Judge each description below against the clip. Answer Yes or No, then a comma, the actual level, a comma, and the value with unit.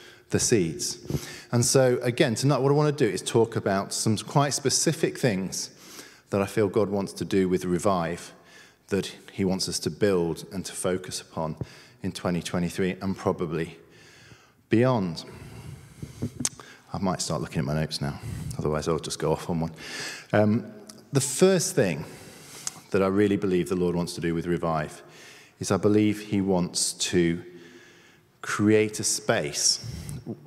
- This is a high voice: No, low, 100 Hz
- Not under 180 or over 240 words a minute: No, average, 160 wpm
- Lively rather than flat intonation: Yes, wide, 6.0 semitones